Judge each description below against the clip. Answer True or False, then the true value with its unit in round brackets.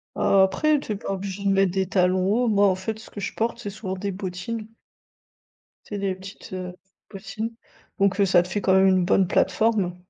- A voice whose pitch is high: True (195 Hz)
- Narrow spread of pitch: True (2.0 semitones)